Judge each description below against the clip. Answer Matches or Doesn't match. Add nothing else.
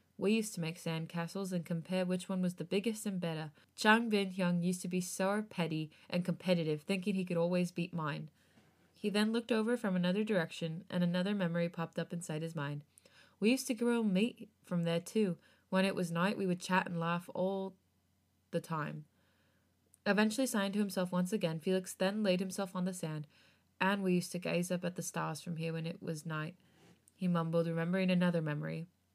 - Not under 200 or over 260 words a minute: Matches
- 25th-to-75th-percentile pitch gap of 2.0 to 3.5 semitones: Matches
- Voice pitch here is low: Doesn't match